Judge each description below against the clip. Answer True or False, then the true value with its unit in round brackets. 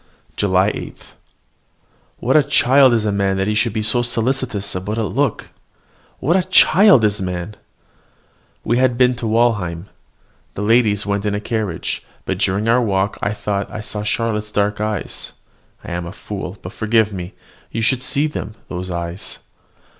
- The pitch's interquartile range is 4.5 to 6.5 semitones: False (3.2 semitones)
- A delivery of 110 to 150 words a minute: False (170 wpm)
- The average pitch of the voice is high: False (105 Hz)